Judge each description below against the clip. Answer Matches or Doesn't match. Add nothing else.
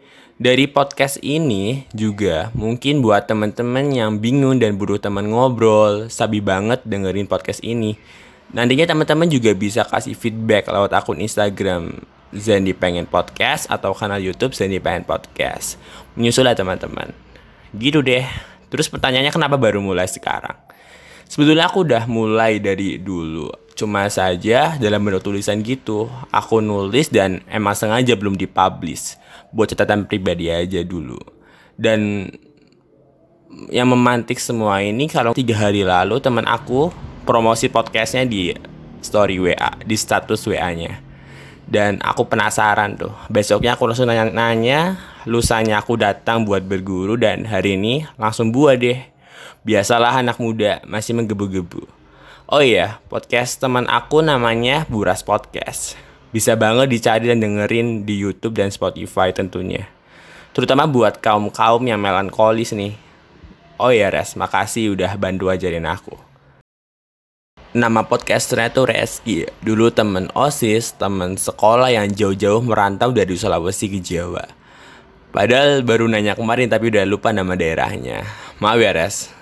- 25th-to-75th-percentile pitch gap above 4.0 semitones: Doesn't match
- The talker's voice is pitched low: Matches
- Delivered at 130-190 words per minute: Matches